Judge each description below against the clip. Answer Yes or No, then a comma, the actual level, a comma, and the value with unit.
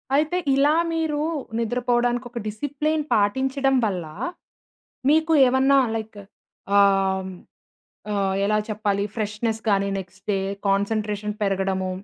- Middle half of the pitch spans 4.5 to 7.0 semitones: Yes, average, 5.1 semitones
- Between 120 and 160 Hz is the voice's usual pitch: No, high, 215 Hz